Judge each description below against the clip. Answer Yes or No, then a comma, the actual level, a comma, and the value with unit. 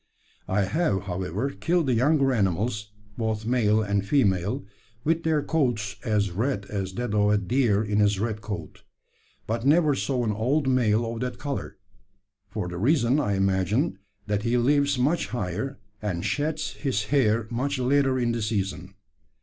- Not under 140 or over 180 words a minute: Yes, average, 165 wpm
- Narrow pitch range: No, average, 4.8 semitones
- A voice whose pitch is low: Yes, low, 115 Hz